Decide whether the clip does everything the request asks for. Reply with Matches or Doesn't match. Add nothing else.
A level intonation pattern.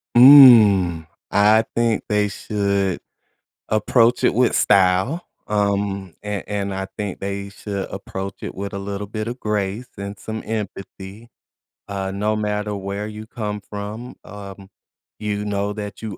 Matches